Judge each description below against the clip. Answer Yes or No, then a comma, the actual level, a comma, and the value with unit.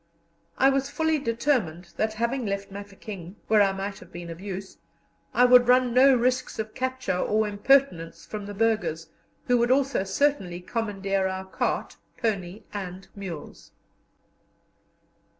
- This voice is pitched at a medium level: No, high, 210 Hz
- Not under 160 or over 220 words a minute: No, average, 145 wpm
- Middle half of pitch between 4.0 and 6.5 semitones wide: Yes, average, 4.7 semitones